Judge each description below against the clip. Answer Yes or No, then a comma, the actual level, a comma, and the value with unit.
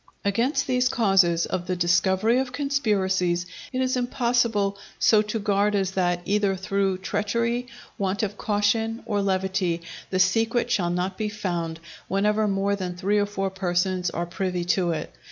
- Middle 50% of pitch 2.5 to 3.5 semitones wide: Yes, average, 2.9 semitones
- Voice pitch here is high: Yes, high, 195 Hz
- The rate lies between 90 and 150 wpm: No, average, 165 wpm